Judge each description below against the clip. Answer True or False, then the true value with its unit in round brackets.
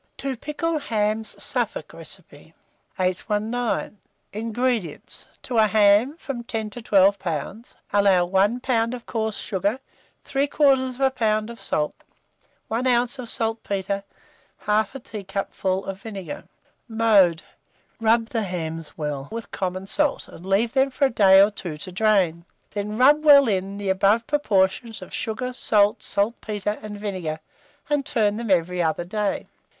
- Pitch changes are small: False (3.6 semitones)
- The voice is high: True (215 Hz)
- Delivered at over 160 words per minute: False (145 wpm)